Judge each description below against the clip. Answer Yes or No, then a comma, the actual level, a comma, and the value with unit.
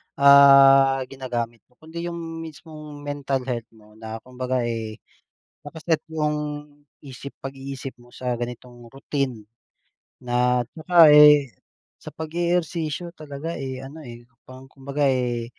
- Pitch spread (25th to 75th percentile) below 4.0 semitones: Yes, average, 3.4 semitones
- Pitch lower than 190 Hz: Yes, low, 135 Hz